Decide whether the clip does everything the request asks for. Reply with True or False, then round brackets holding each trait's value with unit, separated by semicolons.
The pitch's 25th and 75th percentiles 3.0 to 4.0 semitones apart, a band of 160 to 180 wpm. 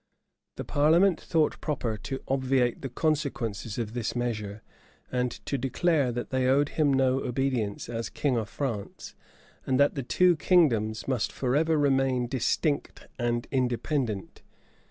False (3.3 semitones; 140 wpm)